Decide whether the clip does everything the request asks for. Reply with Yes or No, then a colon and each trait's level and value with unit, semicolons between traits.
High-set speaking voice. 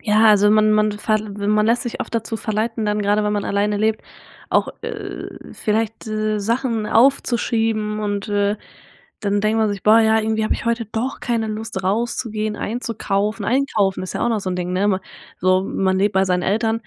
Yes: high, 215 Hz